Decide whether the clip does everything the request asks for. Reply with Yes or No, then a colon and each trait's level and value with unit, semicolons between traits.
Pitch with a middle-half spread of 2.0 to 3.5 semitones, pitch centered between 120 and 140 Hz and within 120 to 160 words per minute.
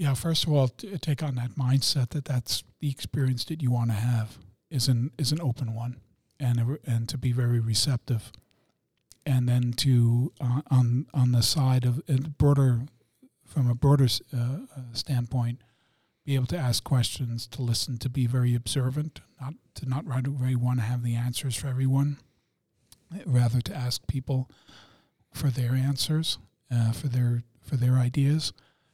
No: narrow, 2.4 semitones; low, 125 Hz; average, 170 wpm